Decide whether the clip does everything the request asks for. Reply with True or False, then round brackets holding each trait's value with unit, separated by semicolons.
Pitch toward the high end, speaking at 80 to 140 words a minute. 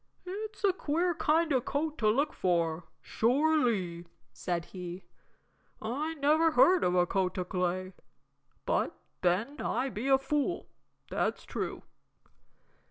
True (255 Hz; 135 wpm)